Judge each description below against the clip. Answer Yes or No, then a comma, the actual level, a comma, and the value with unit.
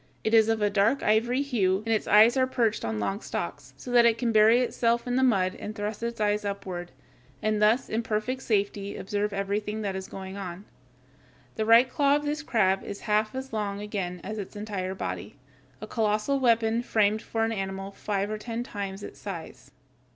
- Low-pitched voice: No, high, 215 Hz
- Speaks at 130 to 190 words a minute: No, average, 200 wpm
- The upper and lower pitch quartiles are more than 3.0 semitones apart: No, narrow, 2.6 semitones